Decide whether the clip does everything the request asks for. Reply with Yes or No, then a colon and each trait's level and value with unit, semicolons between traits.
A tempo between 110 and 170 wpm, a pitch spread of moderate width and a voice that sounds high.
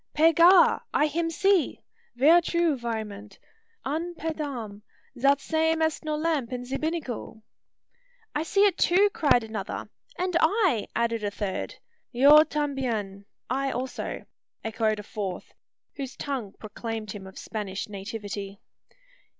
No: slow, 135 wpm; wide, 6.8 semitones; very high, 265 Hz